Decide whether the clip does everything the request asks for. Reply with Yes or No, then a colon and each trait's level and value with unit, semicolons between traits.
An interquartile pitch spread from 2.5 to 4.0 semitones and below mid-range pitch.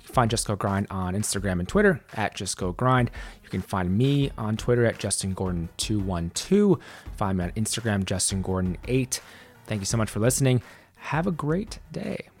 No: average, 4.6 semitones; low, 105 Hz